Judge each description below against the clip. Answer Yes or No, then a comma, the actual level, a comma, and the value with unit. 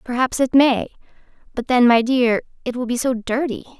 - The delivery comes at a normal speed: Yes, average, 190 wpm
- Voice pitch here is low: No, very high, 250 Hz